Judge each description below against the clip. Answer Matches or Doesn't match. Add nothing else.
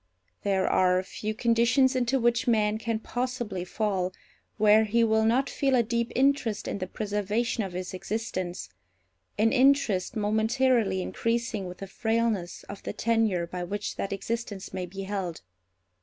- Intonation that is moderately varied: Matches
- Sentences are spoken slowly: Doesn't match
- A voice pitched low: Doesn't match